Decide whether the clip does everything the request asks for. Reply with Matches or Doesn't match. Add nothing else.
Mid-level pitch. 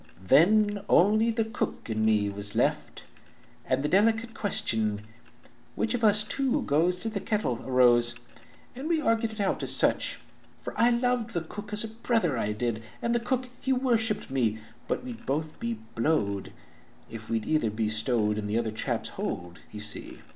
Matches